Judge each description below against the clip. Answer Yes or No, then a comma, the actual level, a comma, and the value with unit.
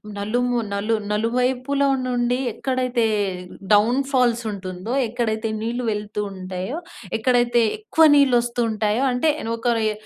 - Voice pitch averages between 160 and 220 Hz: No, high, 240 Hz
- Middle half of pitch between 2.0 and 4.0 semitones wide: Yes, average, 2.8 semitones